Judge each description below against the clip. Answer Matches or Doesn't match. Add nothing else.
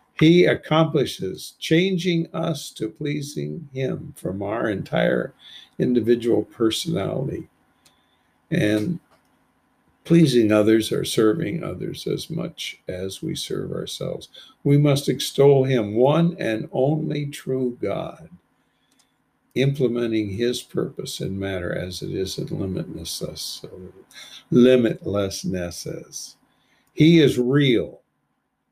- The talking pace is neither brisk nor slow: Doesn't match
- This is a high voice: Doesn't match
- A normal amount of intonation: Doesn't match